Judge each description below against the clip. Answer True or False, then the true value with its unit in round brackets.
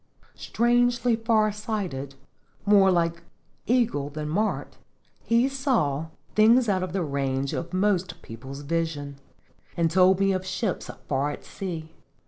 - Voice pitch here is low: False (185 Hz)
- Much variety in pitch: True (6.3 semitones)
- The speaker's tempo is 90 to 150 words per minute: True (135 wpm)